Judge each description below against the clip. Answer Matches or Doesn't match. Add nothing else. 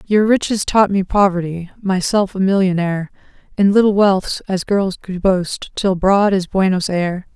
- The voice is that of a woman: Matches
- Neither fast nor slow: Matches